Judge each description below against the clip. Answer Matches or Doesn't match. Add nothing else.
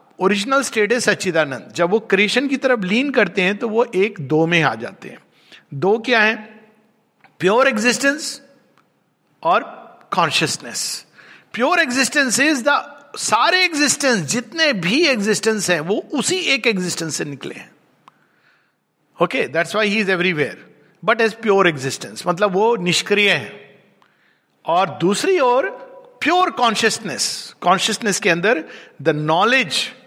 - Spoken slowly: Doesn't match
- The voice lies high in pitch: Matches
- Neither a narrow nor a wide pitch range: Doesn't match